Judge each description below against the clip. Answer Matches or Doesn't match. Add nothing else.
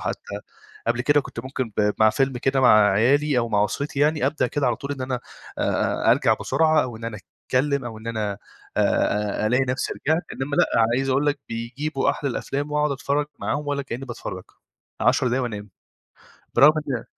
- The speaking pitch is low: Matches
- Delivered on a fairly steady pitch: Doesn't match